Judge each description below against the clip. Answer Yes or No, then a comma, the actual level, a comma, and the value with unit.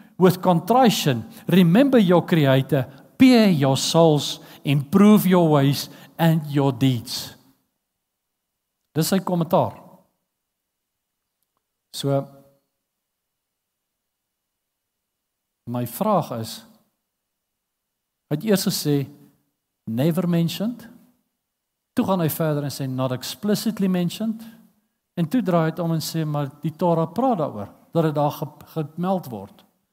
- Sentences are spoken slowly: Yes, slow, 105 wpm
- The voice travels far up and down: Yes, wide, 5.7 semitones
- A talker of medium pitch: Yes, medium, 165 Hz